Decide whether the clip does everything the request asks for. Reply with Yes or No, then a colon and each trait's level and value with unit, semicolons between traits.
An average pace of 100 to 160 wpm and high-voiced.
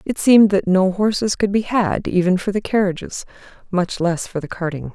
No: fast, 205 wpm; high, 195 Hz